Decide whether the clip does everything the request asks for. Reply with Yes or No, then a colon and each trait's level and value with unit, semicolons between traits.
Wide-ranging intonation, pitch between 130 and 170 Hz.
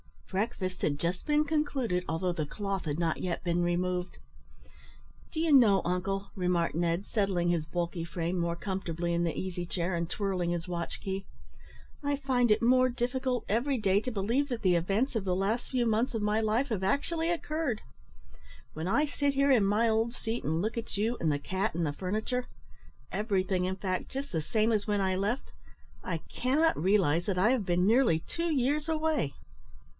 No: wide, 5.8 semitones; high, 200 Hz